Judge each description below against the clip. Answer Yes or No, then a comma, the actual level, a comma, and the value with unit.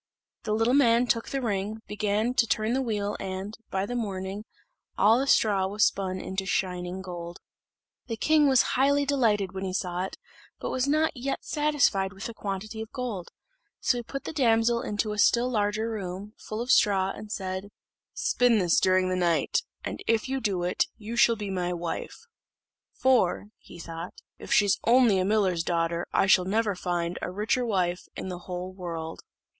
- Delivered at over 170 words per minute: Yes, average, 185 wpm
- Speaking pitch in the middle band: No, high, 205 Hz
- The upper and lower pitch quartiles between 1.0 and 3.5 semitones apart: No, average, 4.0 semitones